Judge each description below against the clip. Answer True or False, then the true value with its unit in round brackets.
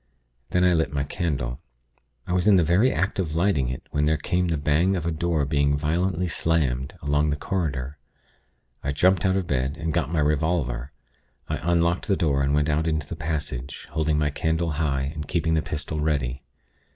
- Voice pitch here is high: False (80 Hz)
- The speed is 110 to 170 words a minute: False (200 wpm)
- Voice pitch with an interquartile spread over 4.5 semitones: False (3.0 semitones)